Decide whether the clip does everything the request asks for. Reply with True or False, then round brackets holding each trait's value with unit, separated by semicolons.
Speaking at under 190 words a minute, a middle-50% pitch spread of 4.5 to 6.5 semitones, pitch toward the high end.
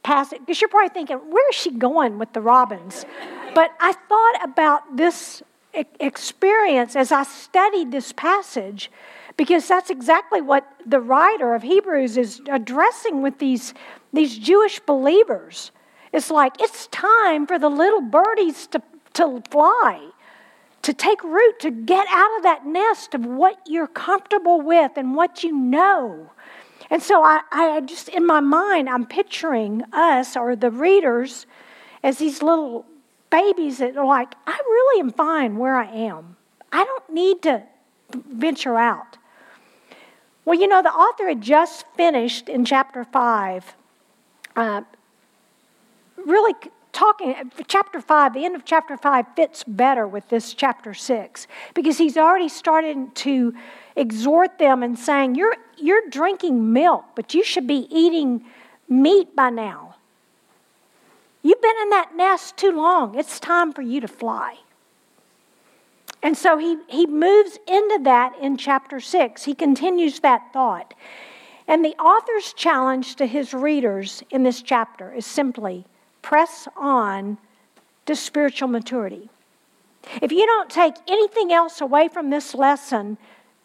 True (145 wpm; 5.3 semitones; 300 Hz)